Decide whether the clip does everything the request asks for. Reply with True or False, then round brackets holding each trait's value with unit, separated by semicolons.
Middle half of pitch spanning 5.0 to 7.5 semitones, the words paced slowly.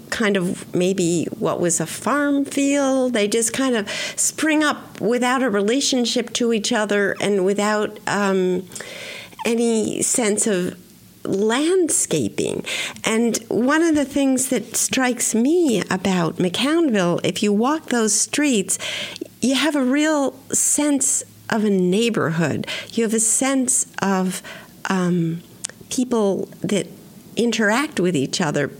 True (5.3 semitones; 130 wpm)